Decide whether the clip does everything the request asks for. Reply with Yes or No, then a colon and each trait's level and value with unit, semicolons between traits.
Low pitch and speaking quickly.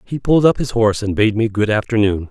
Yes: low, 110 Hz; fast, 260 wpm